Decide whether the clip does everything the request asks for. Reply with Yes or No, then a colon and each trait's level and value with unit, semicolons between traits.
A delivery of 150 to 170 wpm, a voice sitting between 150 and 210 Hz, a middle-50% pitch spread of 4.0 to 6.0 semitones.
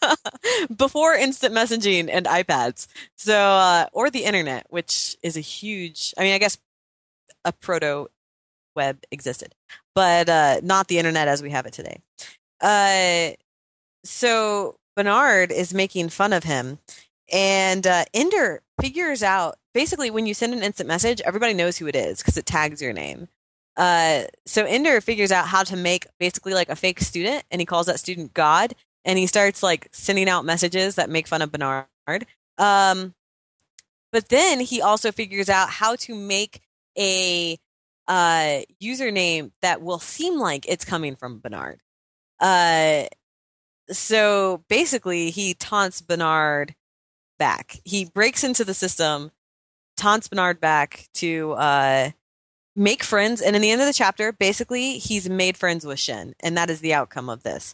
Yes: average, 160 wpm; medium, 185 Hz; average, 4.8 semitones